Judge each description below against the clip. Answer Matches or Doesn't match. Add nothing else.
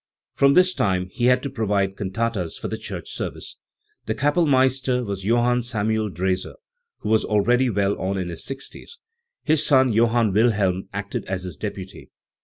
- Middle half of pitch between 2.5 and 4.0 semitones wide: Doesn't match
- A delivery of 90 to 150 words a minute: Doesn't match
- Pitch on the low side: Matches